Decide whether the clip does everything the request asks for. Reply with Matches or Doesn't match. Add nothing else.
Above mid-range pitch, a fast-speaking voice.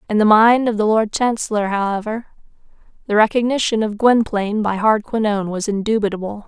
Doesn't match